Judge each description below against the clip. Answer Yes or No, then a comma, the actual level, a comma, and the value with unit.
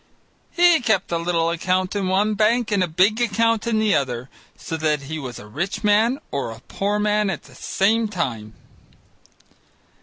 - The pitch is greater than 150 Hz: Yes, high, 190 Hz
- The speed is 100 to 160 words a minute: No, average, 180 wpm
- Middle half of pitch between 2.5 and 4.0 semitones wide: No, wide, 5.4 semitones